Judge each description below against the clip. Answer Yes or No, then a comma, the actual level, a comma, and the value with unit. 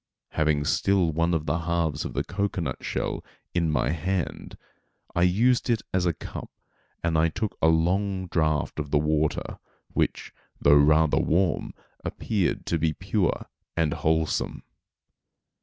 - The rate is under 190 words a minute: Yes, average, 140 wpm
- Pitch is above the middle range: No, very low, 85 Hz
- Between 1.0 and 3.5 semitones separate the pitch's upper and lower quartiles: Yes, average, 3.2 semitones